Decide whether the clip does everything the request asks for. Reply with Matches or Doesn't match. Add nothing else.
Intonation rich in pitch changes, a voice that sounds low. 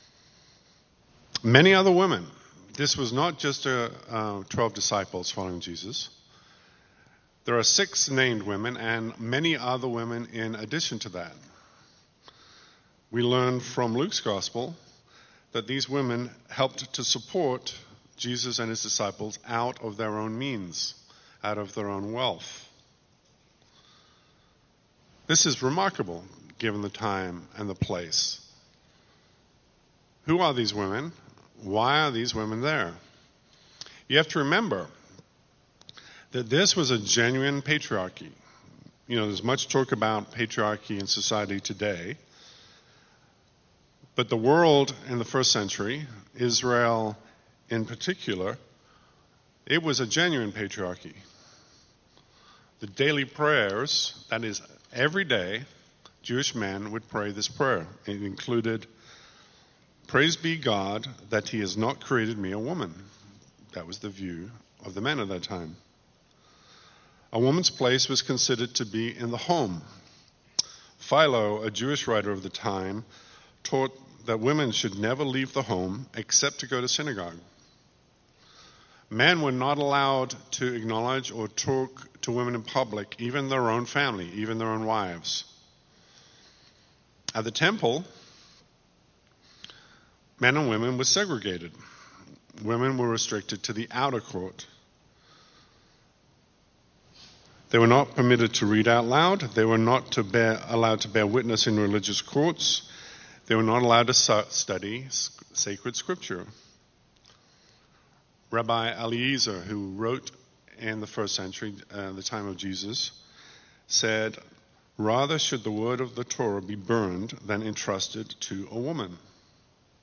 Doesn't match